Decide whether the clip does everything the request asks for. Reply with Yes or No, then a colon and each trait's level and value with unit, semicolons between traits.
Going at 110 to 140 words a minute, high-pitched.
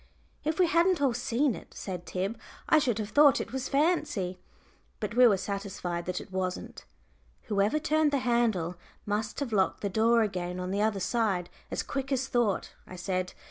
No: average, 185 wpm; high, 220 Hz